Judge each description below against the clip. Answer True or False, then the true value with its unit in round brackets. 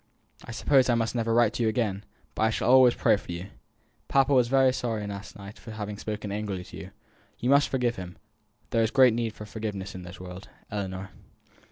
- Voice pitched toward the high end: False (110 Hz)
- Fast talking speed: True (215 wpm)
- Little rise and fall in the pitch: False (3.3 semitones)